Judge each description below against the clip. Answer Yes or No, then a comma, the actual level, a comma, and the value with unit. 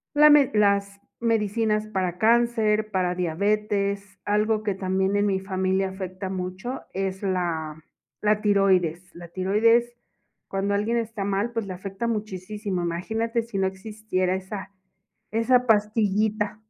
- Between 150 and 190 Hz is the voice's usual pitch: No, high, 200 Hz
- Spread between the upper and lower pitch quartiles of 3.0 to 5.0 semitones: No, narrow, 2.4 semitones